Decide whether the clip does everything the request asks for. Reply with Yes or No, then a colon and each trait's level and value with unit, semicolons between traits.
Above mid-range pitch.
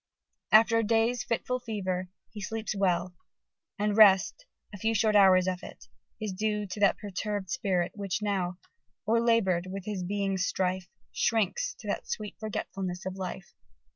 Yes: high, 200 Hz